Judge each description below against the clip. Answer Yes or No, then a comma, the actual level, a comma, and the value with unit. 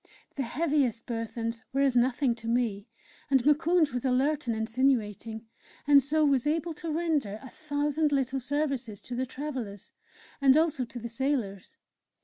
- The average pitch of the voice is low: No, very high, 265 Hz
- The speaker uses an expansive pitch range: No, average, 4.0 semitones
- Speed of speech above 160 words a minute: No, average, 155 wpm